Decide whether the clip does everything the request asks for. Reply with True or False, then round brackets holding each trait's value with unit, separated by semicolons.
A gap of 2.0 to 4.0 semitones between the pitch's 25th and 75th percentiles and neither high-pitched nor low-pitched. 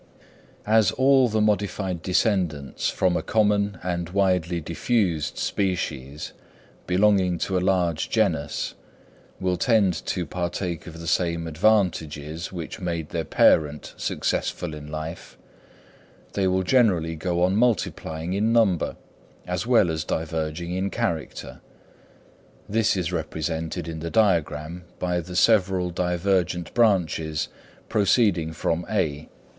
False (3.4 semitones; 90 Hz)